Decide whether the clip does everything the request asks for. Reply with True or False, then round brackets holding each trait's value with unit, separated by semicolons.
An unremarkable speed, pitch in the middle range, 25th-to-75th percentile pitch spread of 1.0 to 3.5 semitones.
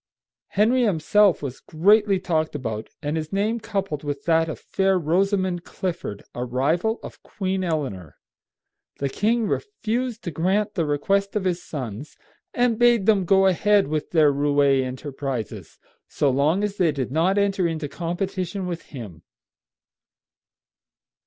False (145 wpm; 175 Hz; 5.5 semitones)